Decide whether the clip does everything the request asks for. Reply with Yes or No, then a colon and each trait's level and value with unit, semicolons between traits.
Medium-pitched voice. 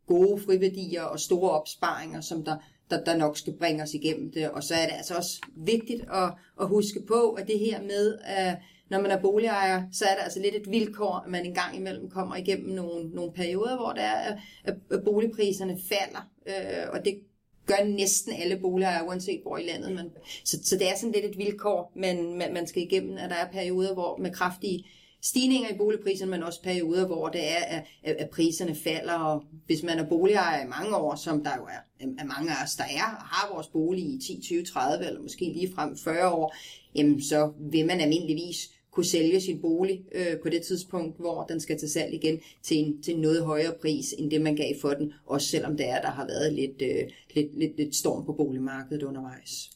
Yes: medium, 175 Hz